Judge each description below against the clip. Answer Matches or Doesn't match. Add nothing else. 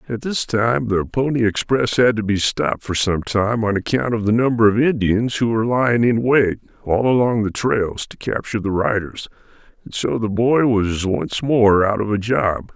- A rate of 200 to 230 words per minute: Matches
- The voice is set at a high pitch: Doesn't match